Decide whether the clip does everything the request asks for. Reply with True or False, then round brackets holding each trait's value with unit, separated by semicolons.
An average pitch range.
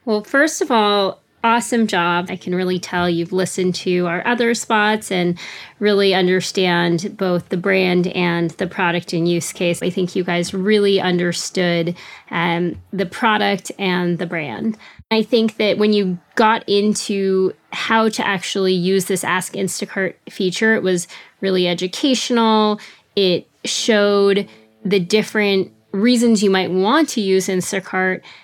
True (3.0 semitones)